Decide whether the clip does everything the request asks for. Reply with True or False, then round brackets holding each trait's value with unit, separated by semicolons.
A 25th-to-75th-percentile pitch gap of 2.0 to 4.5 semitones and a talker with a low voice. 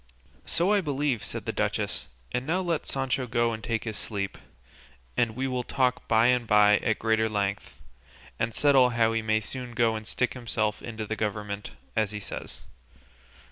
True (2.7 semitones; 115 Hz)